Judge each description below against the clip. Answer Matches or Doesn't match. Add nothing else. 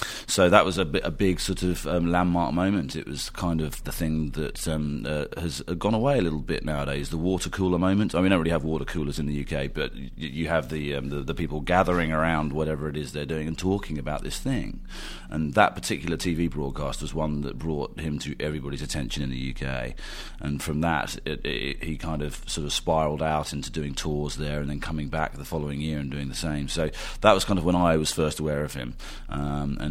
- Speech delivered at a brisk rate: Matches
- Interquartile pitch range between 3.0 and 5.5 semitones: Doesn't match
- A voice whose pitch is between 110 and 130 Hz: Doesn't match